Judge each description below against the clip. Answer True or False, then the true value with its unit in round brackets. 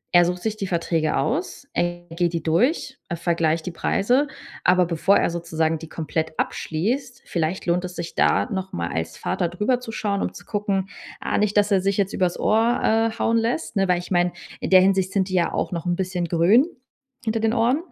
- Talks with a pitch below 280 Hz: True (185 Hz)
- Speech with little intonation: False (4.0 semitones)